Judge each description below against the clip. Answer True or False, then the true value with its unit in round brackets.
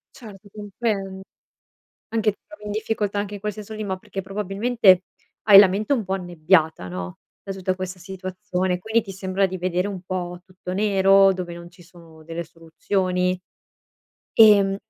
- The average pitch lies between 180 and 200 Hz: True (190 Hz)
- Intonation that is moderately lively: False (2.2 semitones)